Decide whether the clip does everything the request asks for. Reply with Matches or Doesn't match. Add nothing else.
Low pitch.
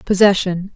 Doesn't match